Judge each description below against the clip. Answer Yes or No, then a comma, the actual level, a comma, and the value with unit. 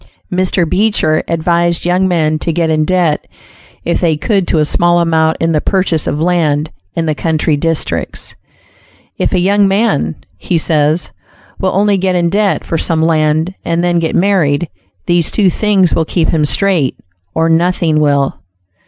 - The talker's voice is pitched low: No, medium, 170 Hz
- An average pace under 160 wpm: No, average, 170 wpm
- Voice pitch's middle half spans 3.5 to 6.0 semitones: No, average, 2.7 semitones